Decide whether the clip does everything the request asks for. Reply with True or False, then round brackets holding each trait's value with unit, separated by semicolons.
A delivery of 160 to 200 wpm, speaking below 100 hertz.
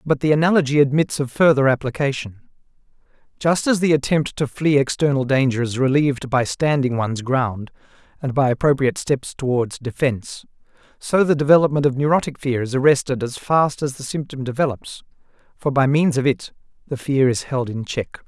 False (170 wpm; 135 Hz)